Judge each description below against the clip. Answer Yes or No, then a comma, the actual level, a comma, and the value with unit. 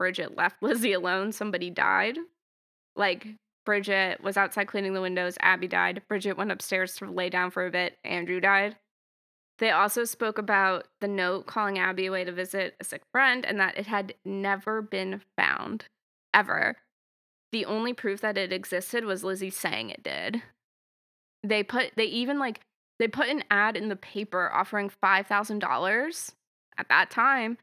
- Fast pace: No, average, 165 wpm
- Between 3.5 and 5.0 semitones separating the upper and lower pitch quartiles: No, narrow, 2.5 semitones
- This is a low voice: No, high, 200 Hz